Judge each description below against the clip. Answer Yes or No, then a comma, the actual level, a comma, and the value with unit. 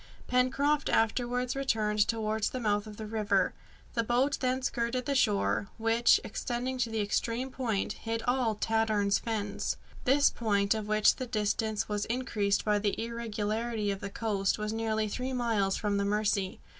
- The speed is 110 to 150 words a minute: No, average, 165 wpm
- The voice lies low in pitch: No, high, 225 Hz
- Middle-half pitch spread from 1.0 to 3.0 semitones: Yes, average, 2.7 semitones